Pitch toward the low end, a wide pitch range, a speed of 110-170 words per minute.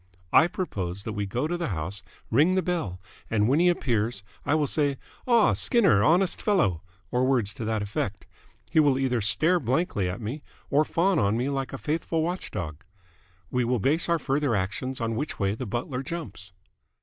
No: low, 130 Hz; wide, 7.5 semitones; average, 190 wpm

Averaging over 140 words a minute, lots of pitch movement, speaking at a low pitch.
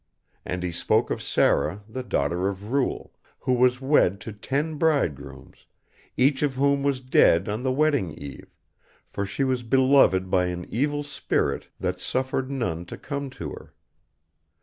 Yes: average, 160 wpm; wide, 6.8 semitones; low, 125 Hz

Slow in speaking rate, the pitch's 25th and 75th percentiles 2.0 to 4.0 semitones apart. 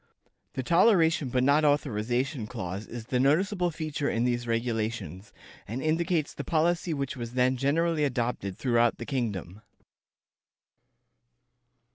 No: slow, 125 wpm; average, 5.0 semitones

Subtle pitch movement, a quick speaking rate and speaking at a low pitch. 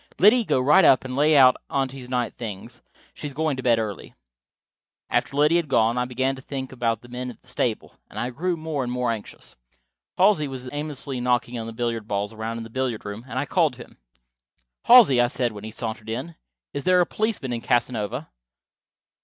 No: average, 3.7 semitones; fast, 210 wpm; low, 125 Hz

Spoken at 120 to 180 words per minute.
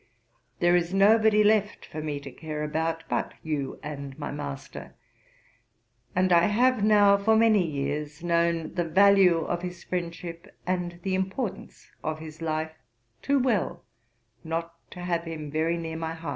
Yes: average, 160 wpm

